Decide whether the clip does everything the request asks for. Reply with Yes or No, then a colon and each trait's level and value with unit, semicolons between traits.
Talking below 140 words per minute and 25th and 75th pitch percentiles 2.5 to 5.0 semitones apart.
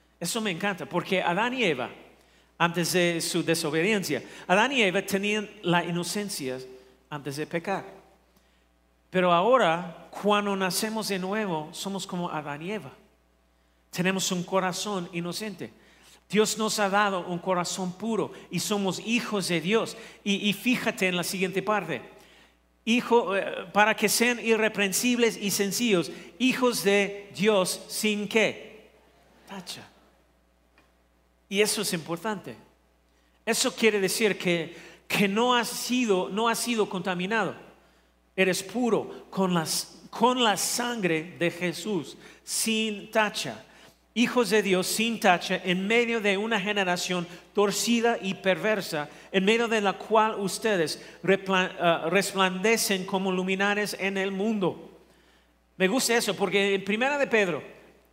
Yes: average, 130 wpm; average, 3.8 semitones